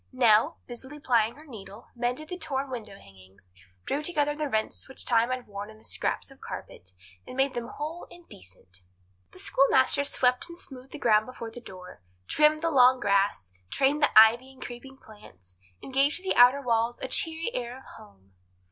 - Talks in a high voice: Yes, very high, 250 Hz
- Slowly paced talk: No, average, 190 wpm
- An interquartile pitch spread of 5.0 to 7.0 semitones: No, average, 4.5 semitones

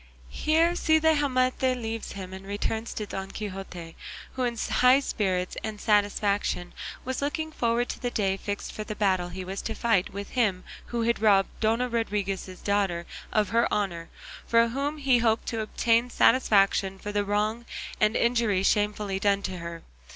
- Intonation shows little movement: No, average, 3.4 semitones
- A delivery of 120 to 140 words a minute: No, average, 170 wpm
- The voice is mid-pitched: No, high, 215 Hz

